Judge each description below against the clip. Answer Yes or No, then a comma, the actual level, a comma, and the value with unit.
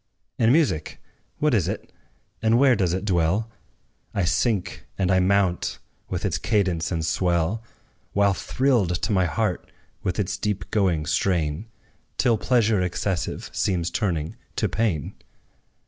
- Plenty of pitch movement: No, average, 4.2 semitones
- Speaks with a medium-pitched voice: No, very low, 95 Hz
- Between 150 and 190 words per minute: No, average, 140 wpm